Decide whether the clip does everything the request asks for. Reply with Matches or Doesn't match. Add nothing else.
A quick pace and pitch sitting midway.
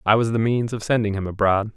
Doesn't match